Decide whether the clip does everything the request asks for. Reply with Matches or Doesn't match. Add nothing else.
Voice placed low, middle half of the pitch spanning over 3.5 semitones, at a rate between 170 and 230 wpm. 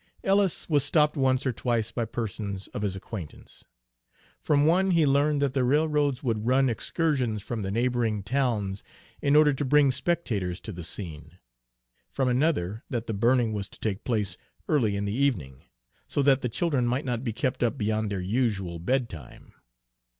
Matches